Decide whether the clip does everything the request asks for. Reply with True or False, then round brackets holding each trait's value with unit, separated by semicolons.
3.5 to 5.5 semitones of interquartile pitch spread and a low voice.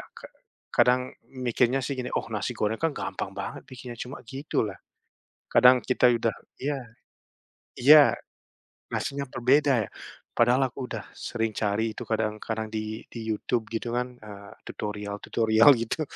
False (2.7 semitones; 120 Hz)